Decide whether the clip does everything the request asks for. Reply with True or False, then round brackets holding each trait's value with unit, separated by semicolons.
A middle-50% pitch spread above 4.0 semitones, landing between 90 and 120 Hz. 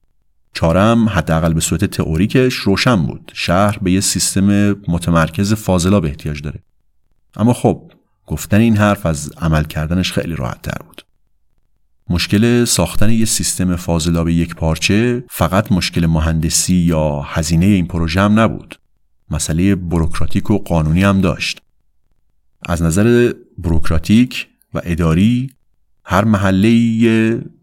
True (4.5 semitones; 95 Hz)